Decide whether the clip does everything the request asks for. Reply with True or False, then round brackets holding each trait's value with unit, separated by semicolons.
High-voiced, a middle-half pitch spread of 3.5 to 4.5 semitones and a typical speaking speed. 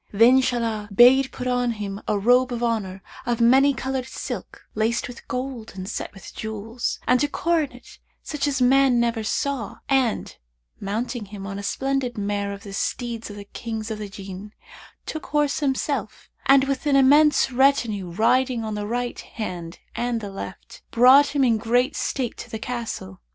True (240 Hz; 3.9 semitones; 175 wpm)